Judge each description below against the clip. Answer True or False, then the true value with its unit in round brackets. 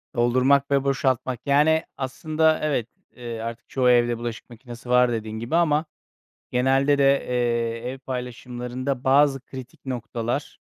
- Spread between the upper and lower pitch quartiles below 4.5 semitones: True (2.5 semitones)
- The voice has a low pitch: True (125 Hz)